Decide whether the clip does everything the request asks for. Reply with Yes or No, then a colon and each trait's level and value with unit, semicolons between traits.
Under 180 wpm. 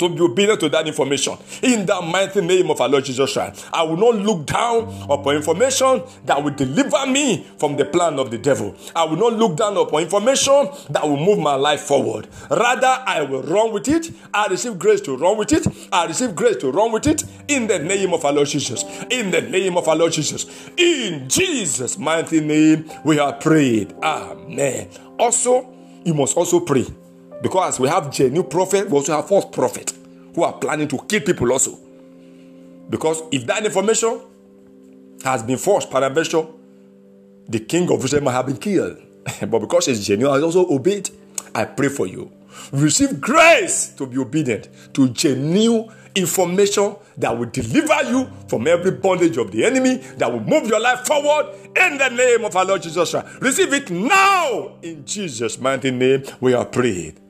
No: average, 185 wpm